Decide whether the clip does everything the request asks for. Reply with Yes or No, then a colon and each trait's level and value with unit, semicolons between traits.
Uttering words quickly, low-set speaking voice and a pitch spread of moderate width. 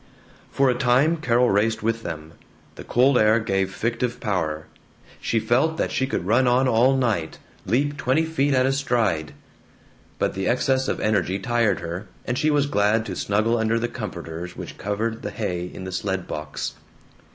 No: average, 180 wpm; low, 115 Hz; average, 4.9 semitones